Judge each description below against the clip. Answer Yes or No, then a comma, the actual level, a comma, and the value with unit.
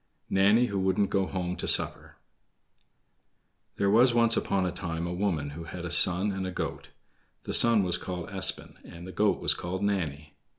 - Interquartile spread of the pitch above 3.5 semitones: No, narrow, 2.5 semitones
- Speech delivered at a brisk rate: No, average, 185 wpm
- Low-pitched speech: Yes, very low, 95 Hz